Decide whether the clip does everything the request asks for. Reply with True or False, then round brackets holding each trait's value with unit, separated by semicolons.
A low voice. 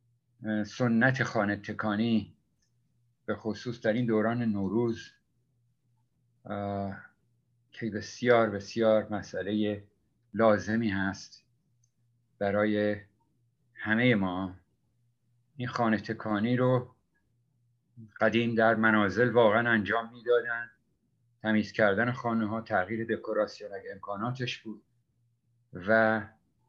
True (115 Hz)